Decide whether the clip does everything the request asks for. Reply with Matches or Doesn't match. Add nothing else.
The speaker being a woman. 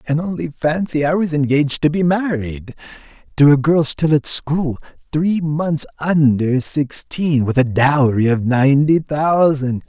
Doesn't match